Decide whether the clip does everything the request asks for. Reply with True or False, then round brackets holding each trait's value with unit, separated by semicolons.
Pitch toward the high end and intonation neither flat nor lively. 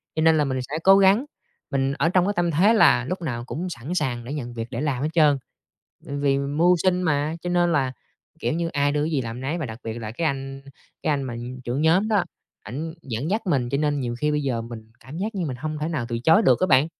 False (145 Hz; 4.5 semitones)